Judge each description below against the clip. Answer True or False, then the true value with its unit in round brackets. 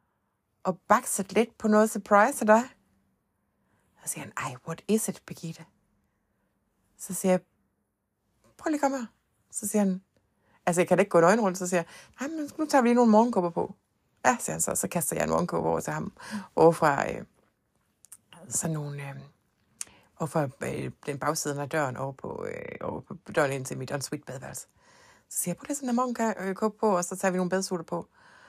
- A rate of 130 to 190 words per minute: True (185 wpm)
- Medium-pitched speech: True (180 Hz)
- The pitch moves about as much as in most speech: False (8.1 semitones)